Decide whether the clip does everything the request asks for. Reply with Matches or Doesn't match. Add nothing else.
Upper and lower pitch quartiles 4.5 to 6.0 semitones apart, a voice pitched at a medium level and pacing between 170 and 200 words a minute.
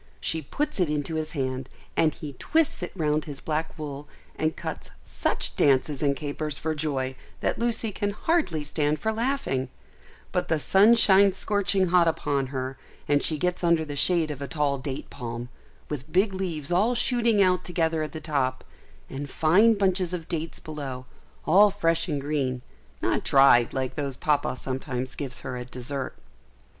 Matches